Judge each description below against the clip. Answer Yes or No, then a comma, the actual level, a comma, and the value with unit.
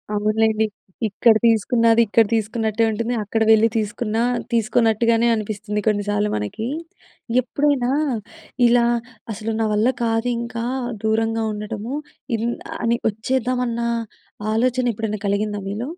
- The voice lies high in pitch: Yes, high, 225 Hz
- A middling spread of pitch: No, narrow, 1.7 semitones